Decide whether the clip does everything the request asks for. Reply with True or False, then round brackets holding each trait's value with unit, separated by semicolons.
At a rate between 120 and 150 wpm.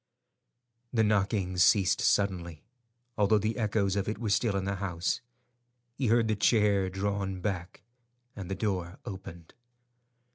True (140 wpm)